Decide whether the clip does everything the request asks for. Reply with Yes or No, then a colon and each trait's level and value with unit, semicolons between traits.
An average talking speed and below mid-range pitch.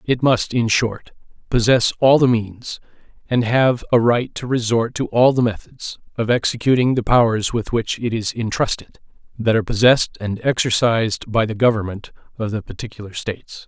Yes: average, 165 wpm; low, 115 Hz